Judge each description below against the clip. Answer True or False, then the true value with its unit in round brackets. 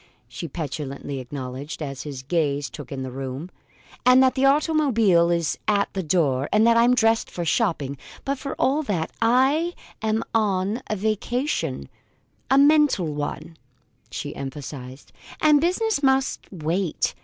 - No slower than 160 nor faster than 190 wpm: False (145 wpm)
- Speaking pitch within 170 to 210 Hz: True (185 Hz)